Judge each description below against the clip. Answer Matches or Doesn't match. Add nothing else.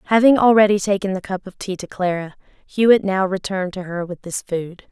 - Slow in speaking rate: Doesn't match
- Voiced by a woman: Matches